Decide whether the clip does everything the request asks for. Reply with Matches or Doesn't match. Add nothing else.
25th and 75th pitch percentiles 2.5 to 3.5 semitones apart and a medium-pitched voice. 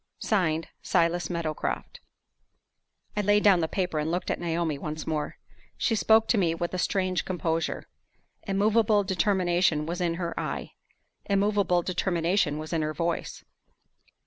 Matches